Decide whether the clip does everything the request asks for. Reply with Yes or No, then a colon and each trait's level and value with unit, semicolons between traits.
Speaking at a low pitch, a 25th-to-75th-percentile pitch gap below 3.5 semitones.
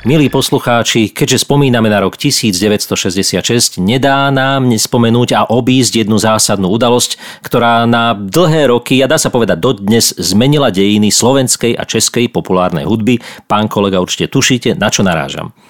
No: low, 120 Hz; average, 3.8 semitones